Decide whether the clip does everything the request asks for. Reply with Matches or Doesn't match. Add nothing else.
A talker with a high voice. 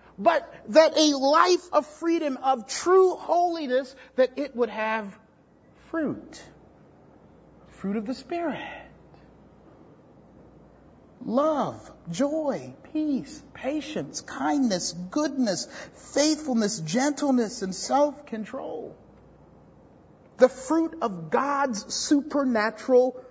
Matches